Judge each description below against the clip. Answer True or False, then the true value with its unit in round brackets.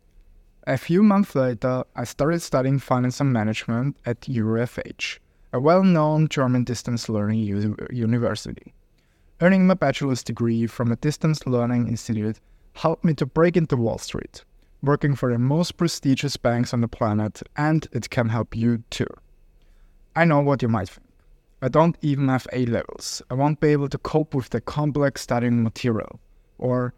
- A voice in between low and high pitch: False (125 Hz)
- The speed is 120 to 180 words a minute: True (165 wpm)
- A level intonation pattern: False (4.1 semitones)